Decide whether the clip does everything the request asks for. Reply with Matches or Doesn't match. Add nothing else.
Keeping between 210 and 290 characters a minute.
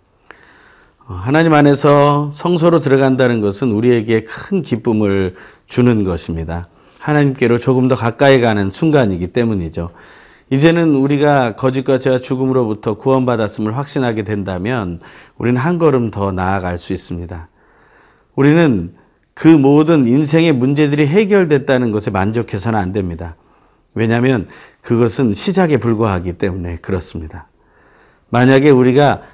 Doesn't match